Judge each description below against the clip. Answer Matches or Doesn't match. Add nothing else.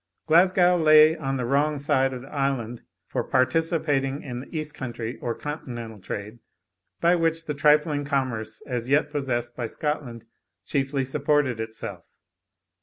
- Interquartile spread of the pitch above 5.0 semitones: Doesn't match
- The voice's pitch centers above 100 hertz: Matches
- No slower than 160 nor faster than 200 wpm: Doesn't match